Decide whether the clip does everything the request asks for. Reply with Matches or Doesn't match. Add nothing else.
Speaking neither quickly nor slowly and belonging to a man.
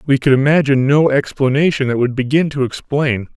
Matches